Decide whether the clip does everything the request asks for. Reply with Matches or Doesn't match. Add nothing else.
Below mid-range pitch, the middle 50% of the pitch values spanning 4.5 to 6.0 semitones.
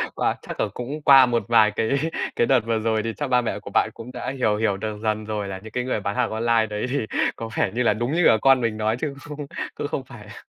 Doesn't match